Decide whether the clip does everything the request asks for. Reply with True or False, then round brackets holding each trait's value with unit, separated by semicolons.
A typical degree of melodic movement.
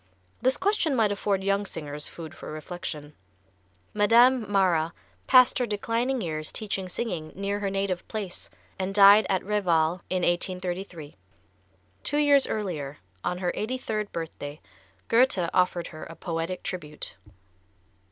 True (4.1 semitones)